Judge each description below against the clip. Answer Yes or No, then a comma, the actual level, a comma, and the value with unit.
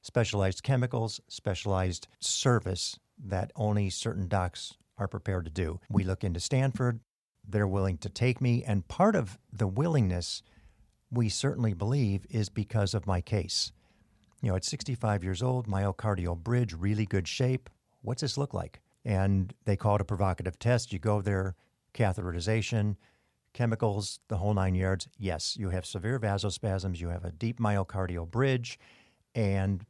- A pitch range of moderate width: Yes, average, 3.5 semitones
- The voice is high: No, low, 105 Hz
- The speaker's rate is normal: Yes, average, 155 wpm